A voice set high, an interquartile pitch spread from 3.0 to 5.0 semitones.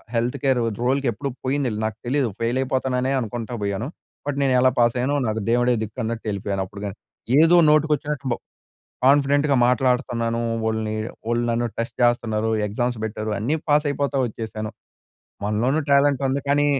No: low, 120 Hz; average, 3.8 semitones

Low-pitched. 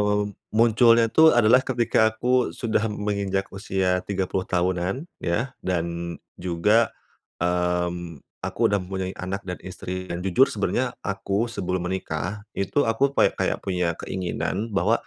Yes: very low, 95 Hz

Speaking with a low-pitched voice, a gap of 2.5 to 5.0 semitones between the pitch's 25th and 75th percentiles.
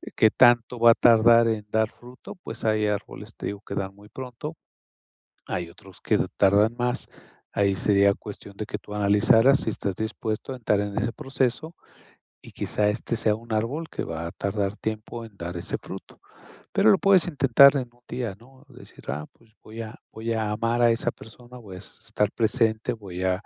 Yes: low, 110 Hz; average, 2.8 semitones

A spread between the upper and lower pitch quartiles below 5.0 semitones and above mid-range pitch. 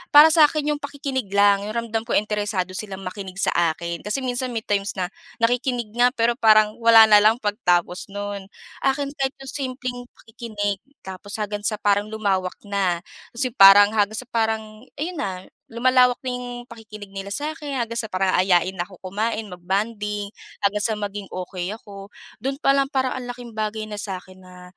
Yes: average, 3.7 semitones; high, 215 Hz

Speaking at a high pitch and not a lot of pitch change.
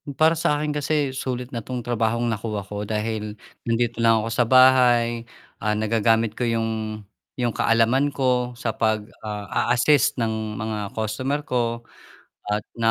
No: low, 115 Hz; narrow, 2.3 semitones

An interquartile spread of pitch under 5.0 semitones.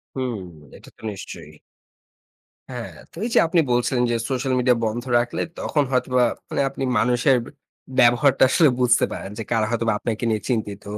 Yes: narrow, 2.5 semitones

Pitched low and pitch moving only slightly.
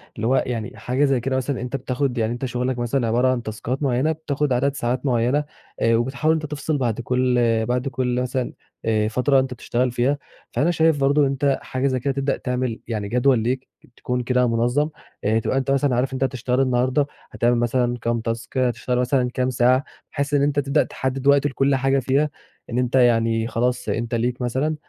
Yes: low, 125 Hz; narrow, 2.2 semitones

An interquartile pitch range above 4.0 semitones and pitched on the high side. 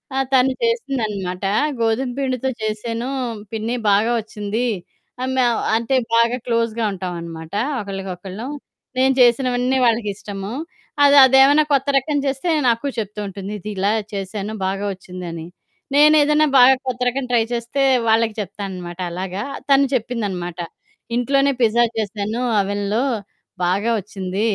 Yes: average, 4.5 semitones; high, 225 Hz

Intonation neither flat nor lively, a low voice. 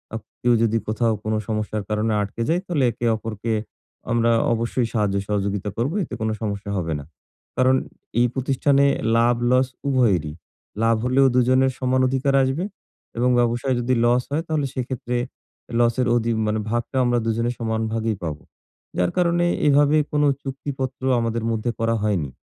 Yes: average, 3.0 semitones; low, 120 Hz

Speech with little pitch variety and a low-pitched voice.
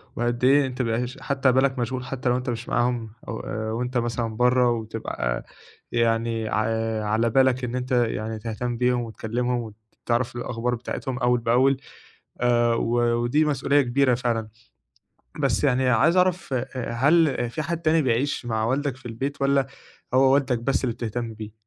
Yes: narrow, 2.3 semitones; low, 125 Hz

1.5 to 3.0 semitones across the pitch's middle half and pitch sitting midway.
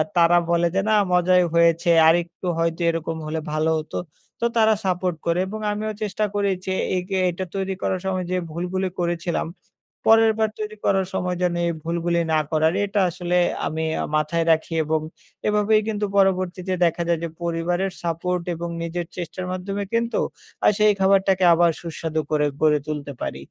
Yes: narrow, 2.5 semitones; medium, 175 Hz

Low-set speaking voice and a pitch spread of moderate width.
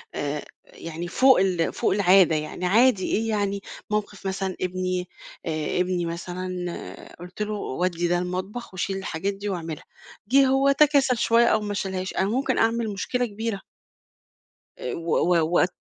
No: high, 190 Hz; average, 3.4 semitones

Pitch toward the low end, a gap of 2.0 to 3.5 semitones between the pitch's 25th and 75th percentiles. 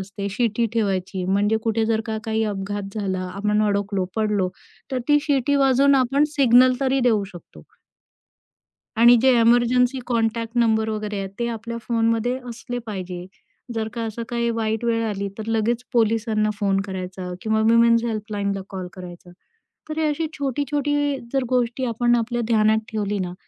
No: high, 225 Hz; average, 3.0 semitones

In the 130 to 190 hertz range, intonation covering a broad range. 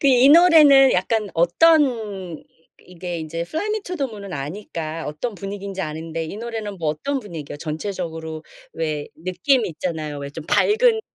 Yes: medium, 185 Hz; wide, 7.5 semitones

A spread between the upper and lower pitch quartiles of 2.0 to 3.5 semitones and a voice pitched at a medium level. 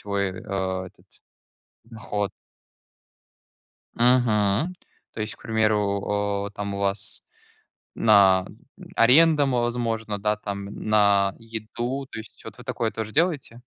No: average, 2.9 semitones; low, 105 Hz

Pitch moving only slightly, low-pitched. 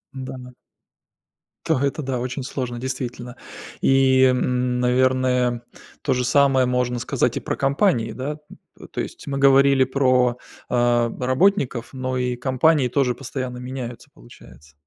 Yes: narrow, 1.5 semitones; low, 130 Hz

